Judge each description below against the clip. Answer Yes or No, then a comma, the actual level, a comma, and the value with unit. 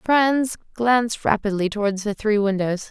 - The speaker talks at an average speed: Yes, average, 145 wpm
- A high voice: Yes, high, 215 Hz